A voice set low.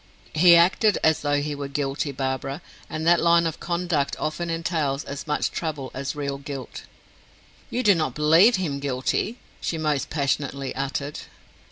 No: medium, 150 Hz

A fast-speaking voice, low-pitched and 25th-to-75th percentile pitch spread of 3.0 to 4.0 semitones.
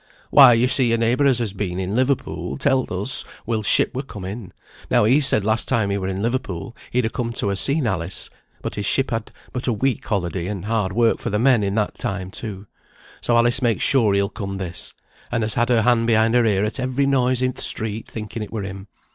Yes: fast, 240 wpm; low, 115 Hz; average, 3.7 semitones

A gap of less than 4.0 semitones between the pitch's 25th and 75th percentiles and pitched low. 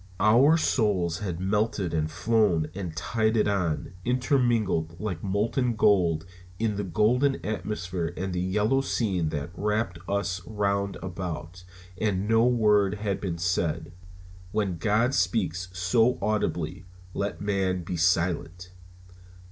Yes: average, 3.5 semitones; low, 100 Hz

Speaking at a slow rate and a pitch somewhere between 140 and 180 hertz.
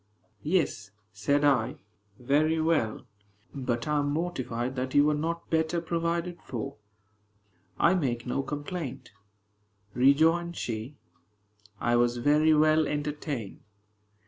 Yes: slow, 115 wpm; medium, 145 Hz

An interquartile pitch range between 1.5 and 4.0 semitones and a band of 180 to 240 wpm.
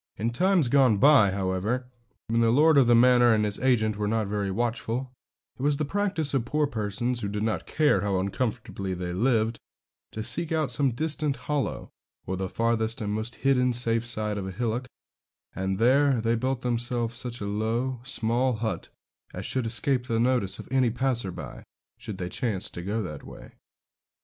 Yes: average, 3.5 semitones; average, 185 wpm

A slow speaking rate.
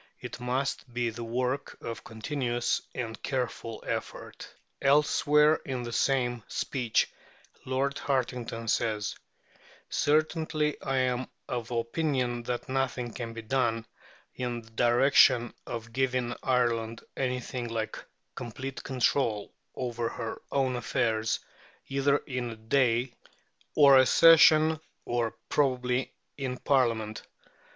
Yes: slow, 115 wpm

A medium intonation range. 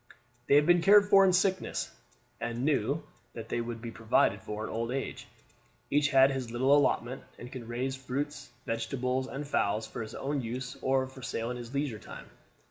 Yes: average, 3.5 semitones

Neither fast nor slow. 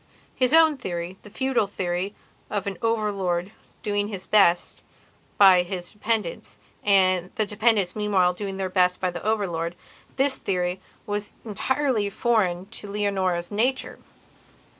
No: slow, 130 wpm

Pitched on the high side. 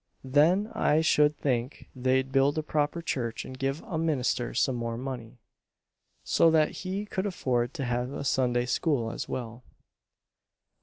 No: low, 135 Hz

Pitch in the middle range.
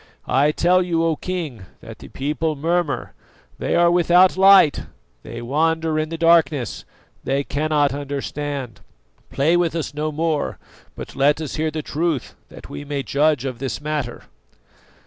Yes: medium, 155 Hz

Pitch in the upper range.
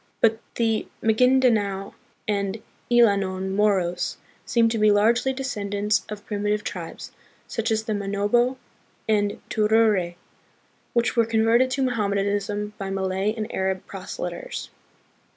Yes: high, 210 Hz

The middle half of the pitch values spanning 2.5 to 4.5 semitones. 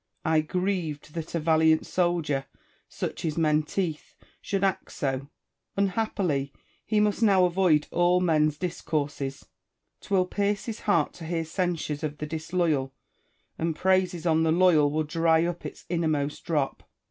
Yes: average, 3.1 semitones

